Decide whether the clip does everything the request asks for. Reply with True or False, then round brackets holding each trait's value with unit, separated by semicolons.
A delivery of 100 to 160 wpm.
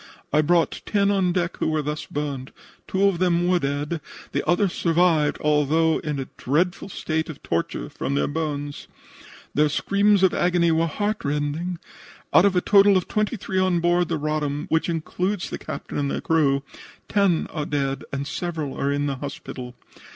False (180 wpm)